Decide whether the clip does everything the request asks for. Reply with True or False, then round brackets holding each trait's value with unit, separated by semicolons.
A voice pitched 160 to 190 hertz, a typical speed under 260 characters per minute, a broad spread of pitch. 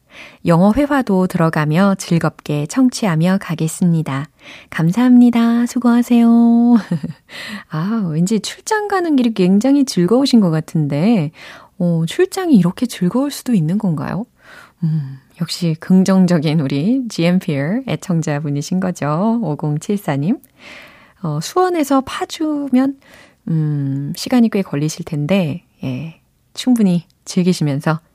True (185 Hz; 250 characters per minute; 7.0 semitones)